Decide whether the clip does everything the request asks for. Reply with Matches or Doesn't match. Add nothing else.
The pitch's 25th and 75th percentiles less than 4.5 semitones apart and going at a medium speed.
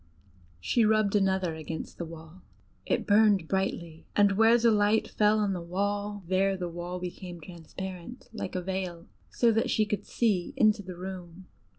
Matches